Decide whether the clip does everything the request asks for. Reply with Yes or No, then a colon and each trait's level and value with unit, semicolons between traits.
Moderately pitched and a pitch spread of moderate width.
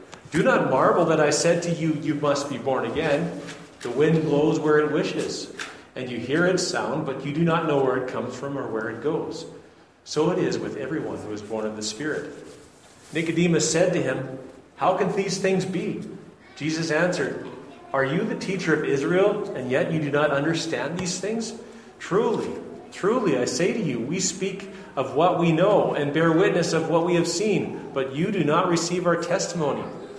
Yes: medium, 160 Hz; average, 3.9 semitones